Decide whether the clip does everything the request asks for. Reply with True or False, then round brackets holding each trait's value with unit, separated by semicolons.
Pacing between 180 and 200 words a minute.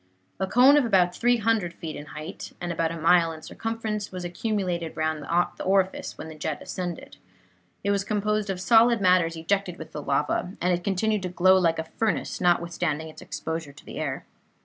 True (195 wpm)